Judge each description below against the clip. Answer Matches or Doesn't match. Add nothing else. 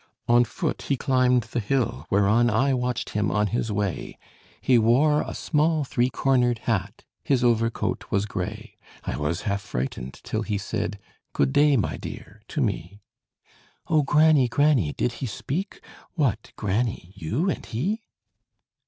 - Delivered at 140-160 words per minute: Matches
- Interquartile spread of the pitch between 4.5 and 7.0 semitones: Matches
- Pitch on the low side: Matches